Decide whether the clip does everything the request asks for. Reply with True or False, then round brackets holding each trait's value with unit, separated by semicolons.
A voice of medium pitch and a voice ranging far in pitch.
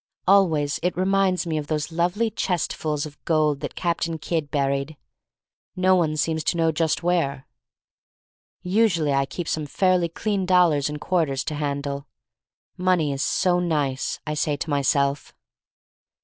False (160 Hz; 3.6 semitones)